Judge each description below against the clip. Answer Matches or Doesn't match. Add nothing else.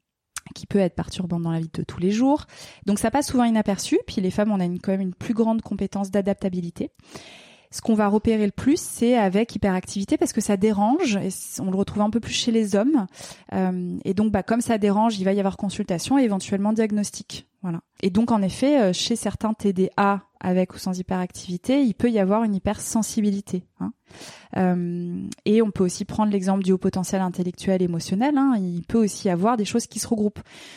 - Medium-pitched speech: Doesn't match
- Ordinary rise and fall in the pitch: Matches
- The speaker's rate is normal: Matches